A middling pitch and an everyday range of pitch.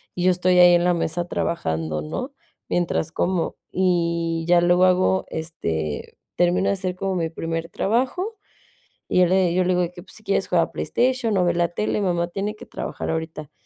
No: medium, 175 Hz; narrow, 2.1 semitones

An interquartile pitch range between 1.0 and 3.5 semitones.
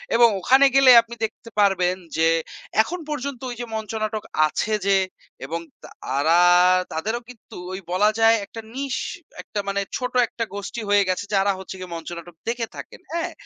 No: average, 4.5 semitones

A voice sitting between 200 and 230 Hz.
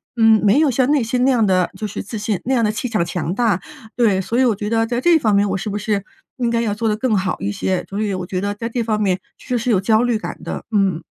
Yes: high, 215 Hz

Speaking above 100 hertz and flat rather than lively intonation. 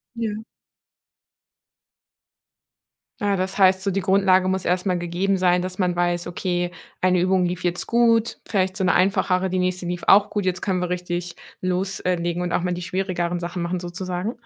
Yes: medium, 185 Hz; narrow, 1.3 semitones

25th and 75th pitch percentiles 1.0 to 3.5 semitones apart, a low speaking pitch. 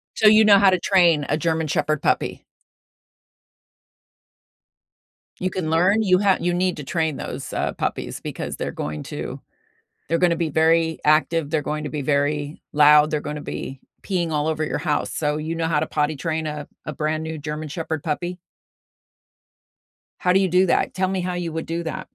No: average, 2.8 semitones; medium, 160 Hz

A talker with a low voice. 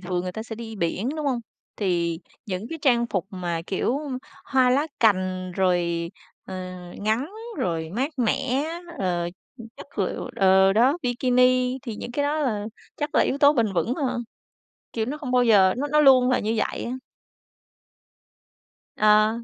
No: high, 225 Hz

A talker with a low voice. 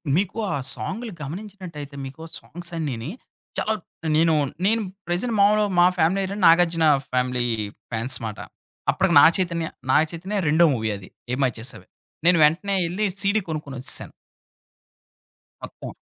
No: medium, 165 Hz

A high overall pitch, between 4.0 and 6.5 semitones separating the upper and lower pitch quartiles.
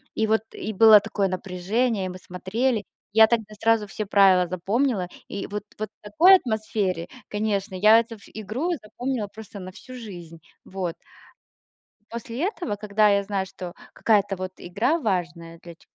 No: high, 210 Hz; average, 3.2 semitones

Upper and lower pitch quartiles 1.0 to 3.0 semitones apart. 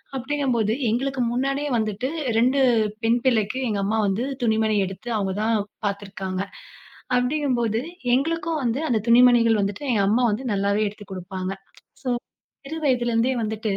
No: average, 3.7 semitones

